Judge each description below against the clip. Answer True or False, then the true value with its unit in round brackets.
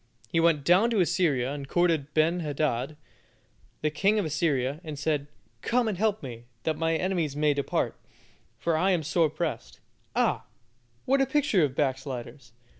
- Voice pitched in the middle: True (155 Hz)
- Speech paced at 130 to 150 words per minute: False (165 wpm)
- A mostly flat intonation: False (3.9 semitones)